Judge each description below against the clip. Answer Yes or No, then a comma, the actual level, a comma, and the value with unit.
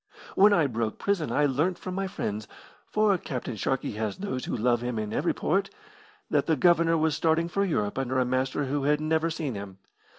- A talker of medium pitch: Yes, medium, 145 Hz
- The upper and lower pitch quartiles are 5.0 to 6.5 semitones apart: Yes, wide, 5.5 semitones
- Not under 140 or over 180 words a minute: No, fast, 205 wpm